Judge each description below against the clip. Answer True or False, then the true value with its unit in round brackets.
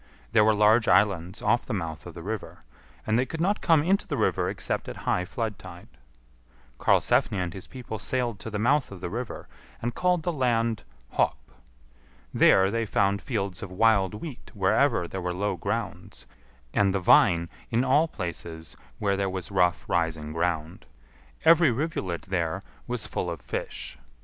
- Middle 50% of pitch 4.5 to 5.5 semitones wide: True (5.0 semitones)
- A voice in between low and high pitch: False (100 Hz)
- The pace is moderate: True (175 wpm)